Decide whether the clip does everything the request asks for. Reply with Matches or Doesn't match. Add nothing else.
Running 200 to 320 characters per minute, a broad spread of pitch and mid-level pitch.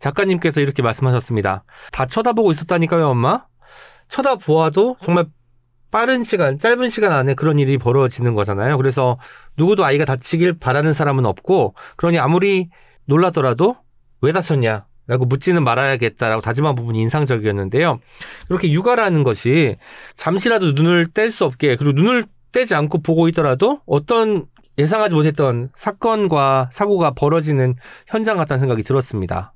Doesn't match